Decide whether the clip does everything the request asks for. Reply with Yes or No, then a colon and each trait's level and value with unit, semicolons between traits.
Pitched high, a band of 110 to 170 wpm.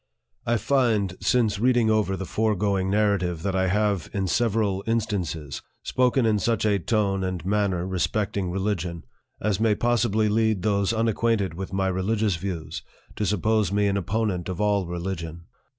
No: low, 100 Hz; average, 155 wpm